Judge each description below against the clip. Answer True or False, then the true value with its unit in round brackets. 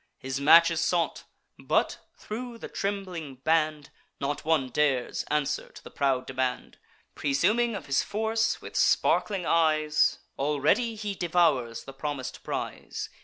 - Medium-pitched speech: True (155 Hz)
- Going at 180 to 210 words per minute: False (135 wpm)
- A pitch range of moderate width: False (5.9 semitones)